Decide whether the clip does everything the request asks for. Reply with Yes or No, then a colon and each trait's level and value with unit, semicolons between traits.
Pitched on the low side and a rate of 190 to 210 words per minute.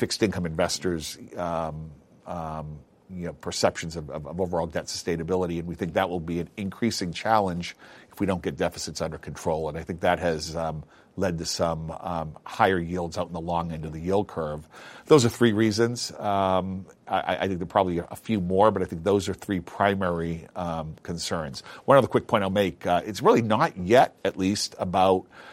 Yes: very low, 90 Hz; average, 200 wpm